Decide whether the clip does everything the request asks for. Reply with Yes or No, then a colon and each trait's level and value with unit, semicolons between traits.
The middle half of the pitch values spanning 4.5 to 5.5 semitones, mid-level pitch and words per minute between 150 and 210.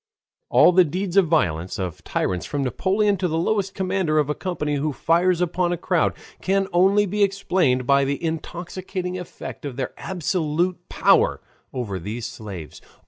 Yes: average, 5.2 semitones; medium, 170 Hz; average, 165 wpm